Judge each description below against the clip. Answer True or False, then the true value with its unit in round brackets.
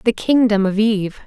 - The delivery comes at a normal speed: True (190 wpm)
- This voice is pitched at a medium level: False (215 Hz)